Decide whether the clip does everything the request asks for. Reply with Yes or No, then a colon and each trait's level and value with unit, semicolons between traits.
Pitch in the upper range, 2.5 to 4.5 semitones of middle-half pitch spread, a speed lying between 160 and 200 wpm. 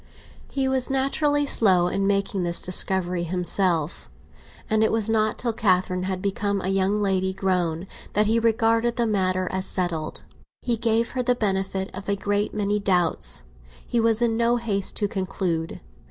Yes: high, 200 Hz; average, 3.4 semitones; average, 170 wpm